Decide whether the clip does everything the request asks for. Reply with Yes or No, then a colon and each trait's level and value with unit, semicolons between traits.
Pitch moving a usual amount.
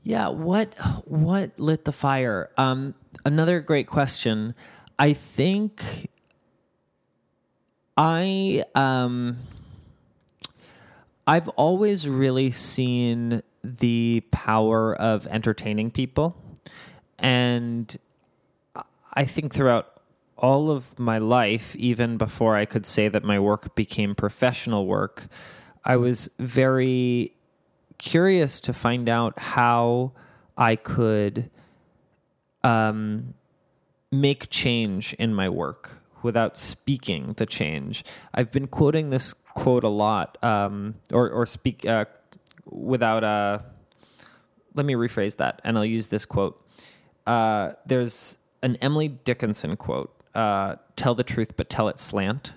Yes: average, 3.7 semitones